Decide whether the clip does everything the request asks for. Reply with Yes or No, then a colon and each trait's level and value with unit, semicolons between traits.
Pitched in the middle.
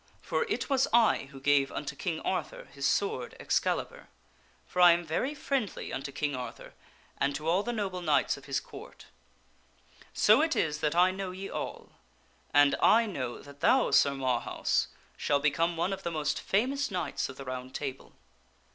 Yes: medium, 160 Hz